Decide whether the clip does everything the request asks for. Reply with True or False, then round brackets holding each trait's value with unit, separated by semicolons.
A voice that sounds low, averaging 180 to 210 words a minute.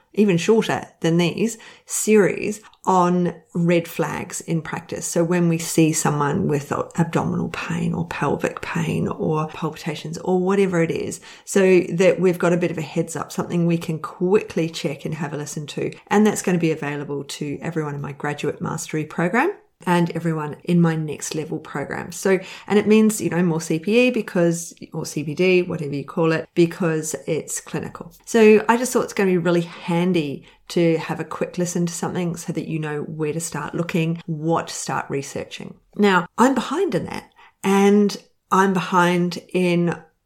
False (170 Hz; 185 wpm)